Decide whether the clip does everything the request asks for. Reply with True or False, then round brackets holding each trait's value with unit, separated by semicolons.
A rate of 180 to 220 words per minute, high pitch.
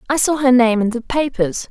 False (245 wpm; 245 Hz)